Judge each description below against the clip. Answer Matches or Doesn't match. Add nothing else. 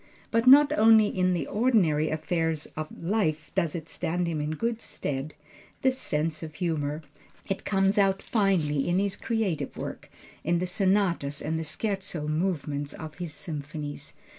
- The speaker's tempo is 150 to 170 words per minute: Matches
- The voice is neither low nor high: Matches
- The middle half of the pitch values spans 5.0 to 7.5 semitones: Doesn't match